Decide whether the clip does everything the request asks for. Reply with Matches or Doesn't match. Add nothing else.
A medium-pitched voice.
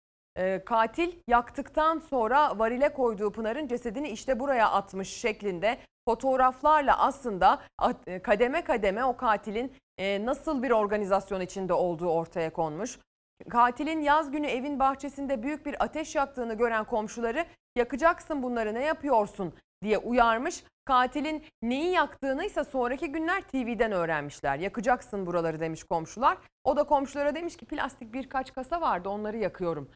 Doesn't match